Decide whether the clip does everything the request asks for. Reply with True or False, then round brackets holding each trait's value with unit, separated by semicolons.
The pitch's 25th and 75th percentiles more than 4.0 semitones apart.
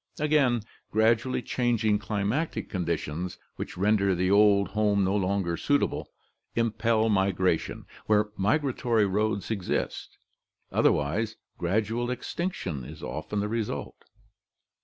False (3.1 semitones)